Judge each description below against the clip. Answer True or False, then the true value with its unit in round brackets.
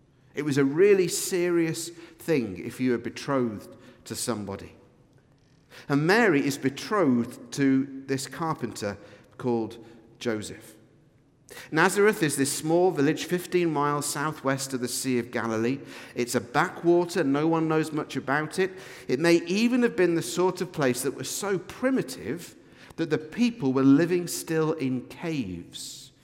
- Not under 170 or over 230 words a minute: False (145 wpm)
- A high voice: False (140 Hz)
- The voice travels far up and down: False (5.0 semitones)